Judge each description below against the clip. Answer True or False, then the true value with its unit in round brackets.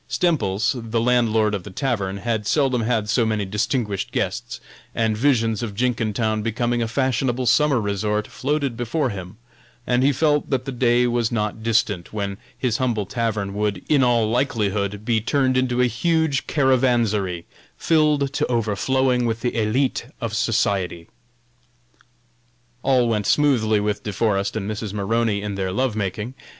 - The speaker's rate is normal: True (155 wpm)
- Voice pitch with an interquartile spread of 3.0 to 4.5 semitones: True (3.3 semitones)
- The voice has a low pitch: True (115 Hz)